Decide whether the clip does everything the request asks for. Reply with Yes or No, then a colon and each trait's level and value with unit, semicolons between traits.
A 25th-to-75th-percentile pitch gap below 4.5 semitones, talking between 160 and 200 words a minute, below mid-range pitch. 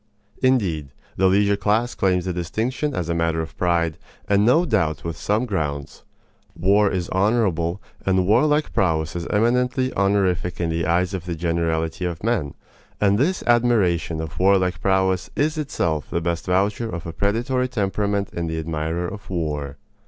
Yes: average, 4.1 semitones; average, 165 wpm; very low, 95 Hz